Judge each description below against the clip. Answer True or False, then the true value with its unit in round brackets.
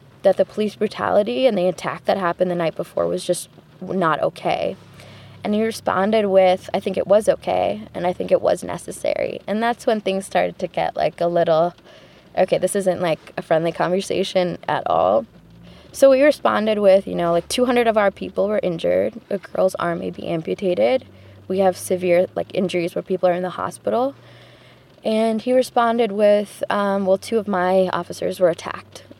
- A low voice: False (190 Hz)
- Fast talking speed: False (190 wpm)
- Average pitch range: True (3.4 semitones)